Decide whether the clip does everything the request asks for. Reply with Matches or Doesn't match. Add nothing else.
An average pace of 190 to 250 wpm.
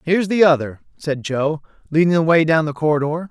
Matches